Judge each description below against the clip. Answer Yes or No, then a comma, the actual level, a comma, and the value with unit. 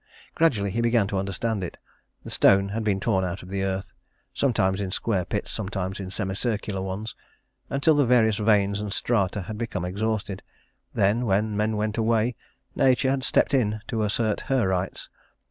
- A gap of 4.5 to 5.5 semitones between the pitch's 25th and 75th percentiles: No, average, 2.8 semitones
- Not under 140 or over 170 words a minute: No, average, 180 wpm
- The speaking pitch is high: No, low, 105 Hz